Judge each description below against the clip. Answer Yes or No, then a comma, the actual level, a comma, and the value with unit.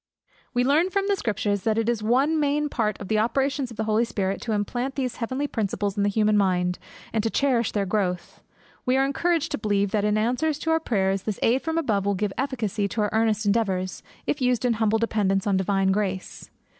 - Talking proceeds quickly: Yes, fast, 220 wpm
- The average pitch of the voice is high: Yes, high, 220 Hz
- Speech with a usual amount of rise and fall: Yes, average, 4.3 semitones